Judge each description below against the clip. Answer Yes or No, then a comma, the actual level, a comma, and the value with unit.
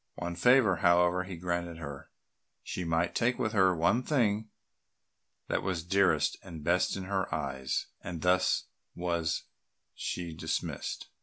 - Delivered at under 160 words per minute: Yes, average, 145 wpm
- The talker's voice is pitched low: Yes, very low, 90 Hz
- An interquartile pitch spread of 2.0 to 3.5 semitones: Yes, narrow, 2.5 semitones